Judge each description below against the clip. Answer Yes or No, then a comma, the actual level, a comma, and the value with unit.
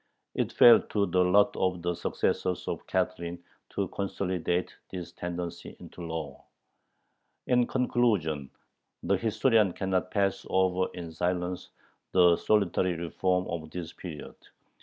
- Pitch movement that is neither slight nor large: No, narrow, 2.0 semitones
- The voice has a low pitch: Yes, very low, 90 Hz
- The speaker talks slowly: Yes, slow, 125 wpm